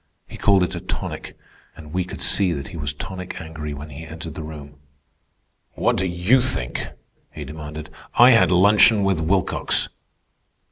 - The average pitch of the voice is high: No, very low, 80 Hz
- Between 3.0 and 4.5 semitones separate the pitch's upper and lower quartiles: Yes, average, 3.9 semitones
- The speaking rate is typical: Yes, average, 170 wpm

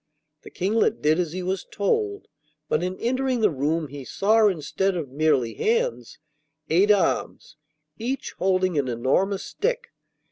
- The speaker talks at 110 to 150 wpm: Yes, average, 145 wpm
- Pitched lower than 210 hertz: Yes, medium, 185 Hz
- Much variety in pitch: Yes, wide, 6.6 semitones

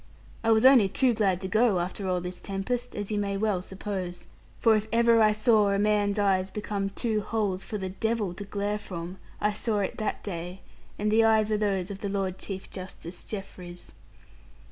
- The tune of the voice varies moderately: No, narrow, 2.3 semitones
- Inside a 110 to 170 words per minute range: No, average, 200 wpm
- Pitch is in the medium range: No, high, 205 Hz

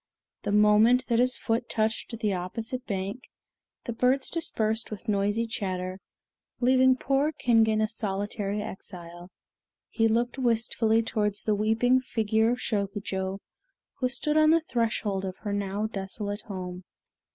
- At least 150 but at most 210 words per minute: No, average, 140 wpm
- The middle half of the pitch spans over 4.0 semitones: No, average, 3.1 semitones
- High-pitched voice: Yes, high, 220 Hz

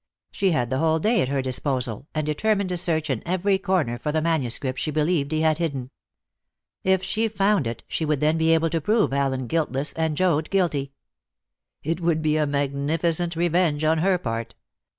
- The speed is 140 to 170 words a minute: No, average, 190 wpm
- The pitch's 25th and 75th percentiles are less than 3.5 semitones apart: No, average, 3.8 semitones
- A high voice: No, medium, 155 Hz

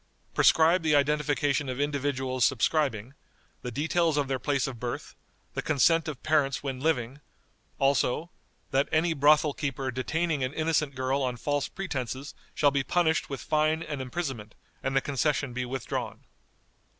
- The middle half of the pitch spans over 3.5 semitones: No, average, 2.9 semitones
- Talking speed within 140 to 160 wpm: Yes, average, 150 wpm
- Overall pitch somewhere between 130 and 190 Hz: Yes, medium, 140 Hz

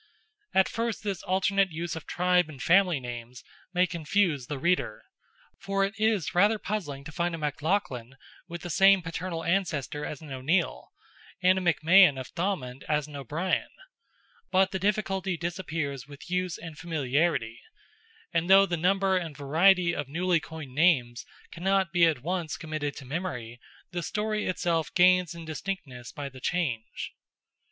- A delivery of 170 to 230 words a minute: No, average, 155 wpm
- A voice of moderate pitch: Yes, medium, 170 Hz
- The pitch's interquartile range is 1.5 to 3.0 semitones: No, average, 4.2 semitones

